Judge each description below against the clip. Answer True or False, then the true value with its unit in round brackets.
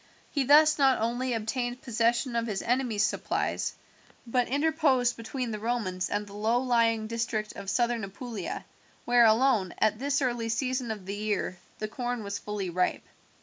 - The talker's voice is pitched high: True (230 Hz)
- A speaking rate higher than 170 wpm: False (165 wpm)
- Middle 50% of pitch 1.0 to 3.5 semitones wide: True (2.9 semitones)